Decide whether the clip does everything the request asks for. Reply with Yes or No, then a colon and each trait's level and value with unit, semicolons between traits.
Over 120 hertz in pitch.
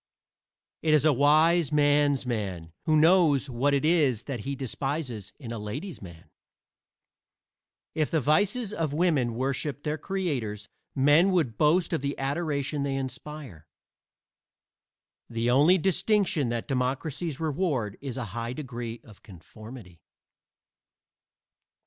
Yes: medium, 140 Hz